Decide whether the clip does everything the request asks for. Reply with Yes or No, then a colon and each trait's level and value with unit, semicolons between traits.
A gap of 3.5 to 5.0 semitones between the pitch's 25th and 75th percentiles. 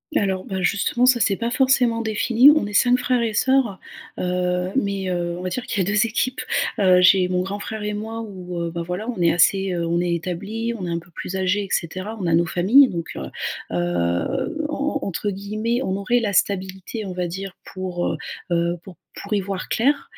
Yes: average, 4.0 semitones